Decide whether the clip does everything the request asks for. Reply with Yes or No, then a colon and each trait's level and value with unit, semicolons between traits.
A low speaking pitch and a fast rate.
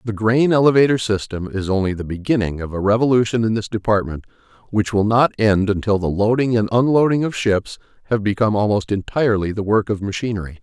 No: low, 110 Hz; average, 185 wpm